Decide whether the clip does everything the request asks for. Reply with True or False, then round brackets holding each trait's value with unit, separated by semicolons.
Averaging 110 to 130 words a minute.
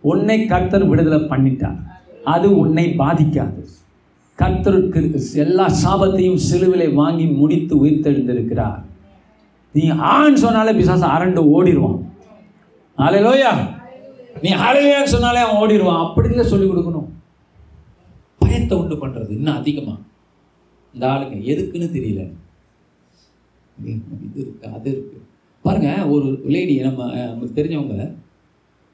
False (100 wpm)